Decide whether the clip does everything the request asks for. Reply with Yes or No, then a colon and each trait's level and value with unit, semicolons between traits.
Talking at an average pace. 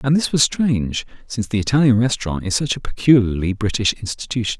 Yes: average, 185 wpm